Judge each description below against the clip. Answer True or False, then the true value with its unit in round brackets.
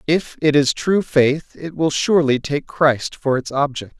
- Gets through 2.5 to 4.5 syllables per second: True (4.3 syllables/s)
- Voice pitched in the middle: True (145 Hz)